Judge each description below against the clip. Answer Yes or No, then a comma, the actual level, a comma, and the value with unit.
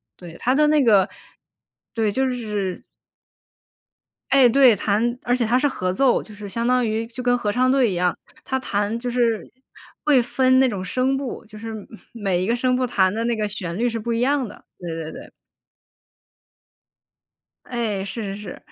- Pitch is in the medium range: No, high, 230 Hz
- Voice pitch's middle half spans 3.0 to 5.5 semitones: Yes, average, 3.6 semitones